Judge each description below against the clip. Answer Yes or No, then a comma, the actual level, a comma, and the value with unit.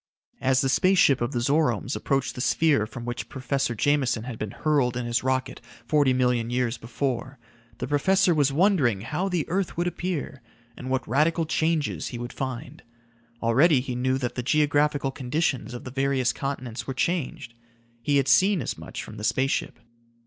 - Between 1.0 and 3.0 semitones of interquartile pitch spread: No, average, 3.5 semitones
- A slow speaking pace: No, average, 185 wpm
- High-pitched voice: No, low, 135 Hz